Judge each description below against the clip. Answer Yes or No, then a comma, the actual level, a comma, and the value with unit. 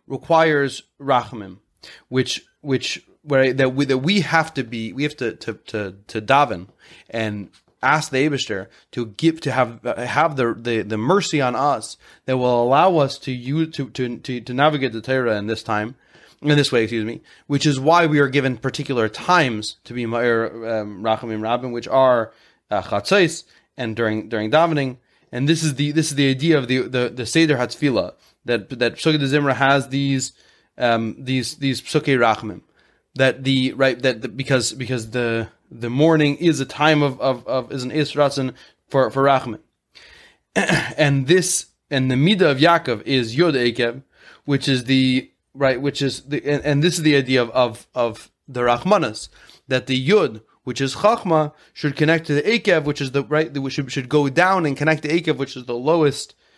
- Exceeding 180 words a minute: Yes, average, 190 wpm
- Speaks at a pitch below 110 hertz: No, low, 135 Hz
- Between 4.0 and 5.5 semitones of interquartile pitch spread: No, average, 3.6 semitones